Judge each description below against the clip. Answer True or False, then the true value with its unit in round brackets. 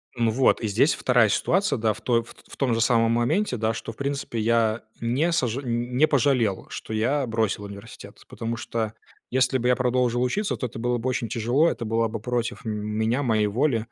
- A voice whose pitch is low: True (120 Hz)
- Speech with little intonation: True (2.3 semitones)